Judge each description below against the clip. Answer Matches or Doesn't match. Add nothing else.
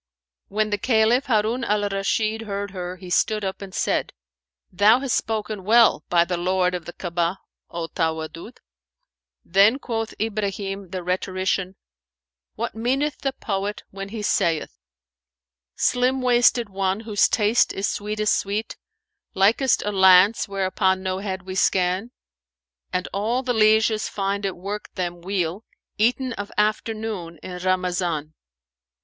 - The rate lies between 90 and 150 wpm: Matches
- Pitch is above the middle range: Matches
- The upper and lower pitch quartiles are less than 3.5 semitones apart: Matches